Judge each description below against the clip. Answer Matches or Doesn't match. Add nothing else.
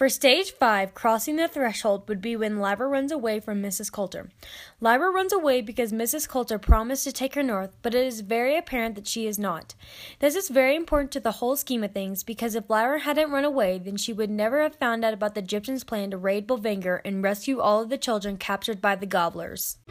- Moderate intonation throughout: Matches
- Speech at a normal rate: Doesn't match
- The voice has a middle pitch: Doesn't match